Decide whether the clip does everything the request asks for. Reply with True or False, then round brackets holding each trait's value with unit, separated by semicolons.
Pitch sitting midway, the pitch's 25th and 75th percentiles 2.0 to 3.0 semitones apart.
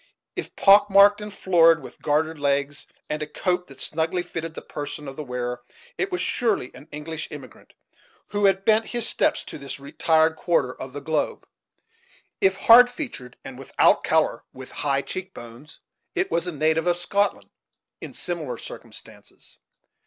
False (160 Hz; 5.4 semitones)